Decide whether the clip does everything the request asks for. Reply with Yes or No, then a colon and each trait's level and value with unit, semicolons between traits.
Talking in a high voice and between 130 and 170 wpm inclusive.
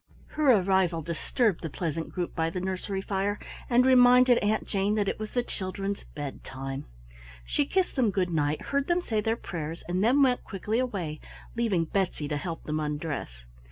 No: high, 195 Hz; average, 180 wpm